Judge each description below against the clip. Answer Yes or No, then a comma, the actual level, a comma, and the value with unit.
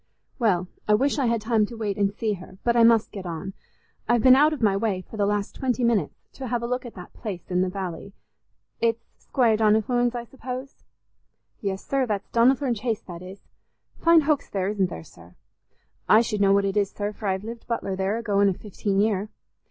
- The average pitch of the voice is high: Yes, high, 215 Hz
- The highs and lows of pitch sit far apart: No, average, 3.3 semitones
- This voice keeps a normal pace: No, fast, 220 wpm